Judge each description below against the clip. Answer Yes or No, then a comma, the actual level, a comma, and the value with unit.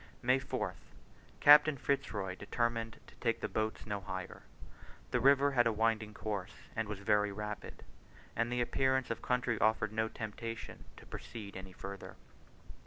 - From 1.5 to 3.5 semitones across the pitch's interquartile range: Yes, average, 2.9 semitones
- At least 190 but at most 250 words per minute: No, average, 165 wpm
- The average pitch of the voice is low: Yes, low, 110 Hz